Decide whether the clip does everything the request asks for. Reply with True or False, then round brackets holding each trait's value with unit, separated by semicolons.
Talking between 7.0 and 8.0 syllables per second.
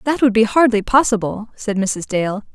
False (4.8 syllables/s)